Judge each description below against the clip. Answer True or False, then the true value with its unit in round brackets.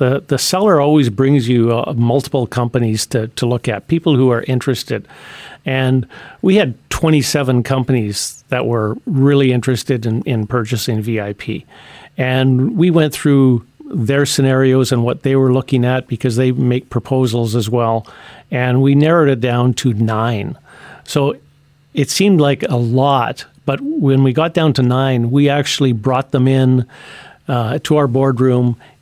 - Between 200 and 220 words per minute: False (160 wpm)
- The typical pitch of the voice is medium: False (130 Hz)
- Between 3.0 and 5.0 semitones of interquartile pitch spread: False (2.4 semitones)